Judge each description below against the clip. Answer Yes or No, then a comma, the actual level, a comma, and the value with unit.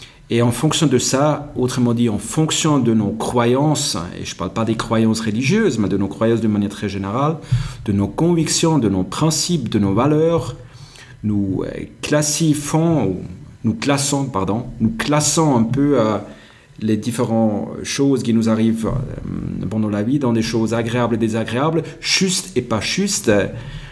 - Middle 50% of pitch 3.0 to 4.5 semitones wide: No, average, 5.1 semitones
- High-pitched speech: No, low, 125 Hz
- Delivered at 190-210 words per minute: No, average, 165 wpm